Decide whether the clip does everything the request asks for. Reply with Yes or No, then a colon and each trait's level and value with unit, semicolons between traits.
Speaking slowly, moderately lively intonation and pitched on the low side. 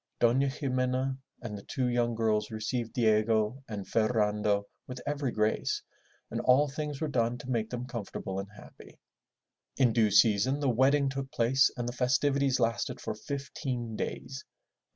No: average, 155 wpm; average, 3.4 semitones; low, 125 Hz